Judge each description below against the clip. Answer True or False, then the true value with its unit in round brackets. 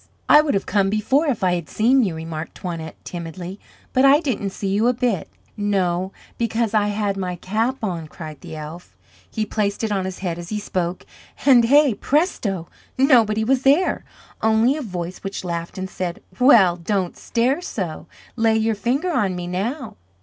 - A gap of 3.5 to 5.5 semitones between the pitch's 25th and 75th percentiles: True (5.1 semitones)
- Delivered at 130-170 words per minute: False (185 wpm)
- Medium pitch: False (205 Hz)